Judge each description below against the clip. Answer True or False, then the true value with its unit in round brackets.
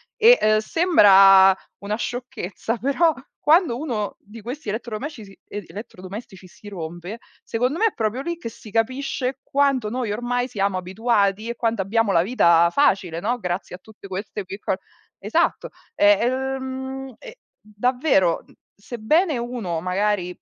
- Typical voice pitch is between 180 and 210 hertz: False (220 Hz)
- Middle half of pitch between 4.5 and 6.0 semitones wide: True (4.8 semitones)